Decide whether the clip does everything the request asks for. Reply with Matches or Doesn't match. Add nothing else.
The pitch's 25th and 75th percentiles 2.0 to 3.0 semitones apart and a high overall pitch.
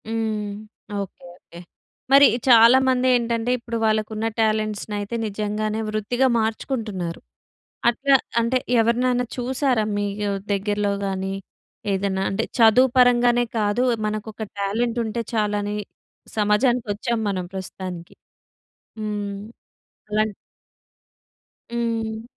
Matches